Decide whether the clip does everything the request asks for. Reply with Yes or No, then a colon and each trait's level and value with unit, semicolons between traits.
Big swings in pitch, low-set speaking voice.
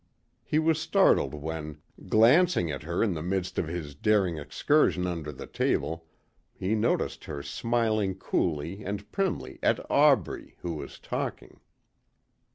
Yes: wide, 6.2 semitones; very low, 90 Hz